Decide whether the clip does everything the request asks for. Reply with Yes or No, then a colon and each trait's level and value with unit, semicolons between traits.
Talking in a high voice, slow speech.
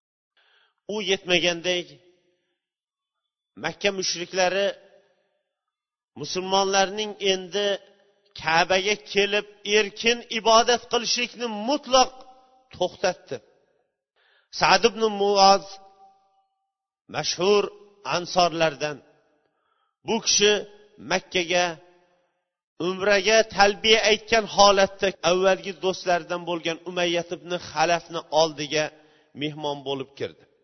Yes: high, 195 Hz; slow, 70 wpm